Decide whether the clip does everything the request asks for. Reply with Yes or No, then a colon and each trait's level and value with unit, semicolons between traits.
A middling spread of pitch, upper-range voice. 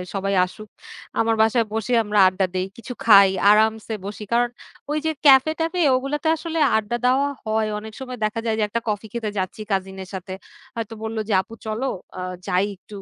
Yes: average, 3.2 semitones; high, 220 Hz